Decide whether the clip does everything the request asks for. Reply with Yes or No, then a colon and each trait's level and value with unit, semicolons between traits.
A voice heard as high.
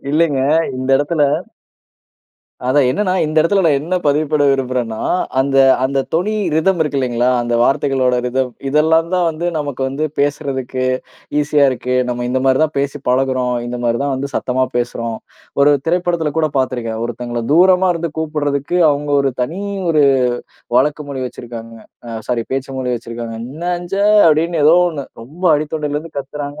No: medium, 140 Hz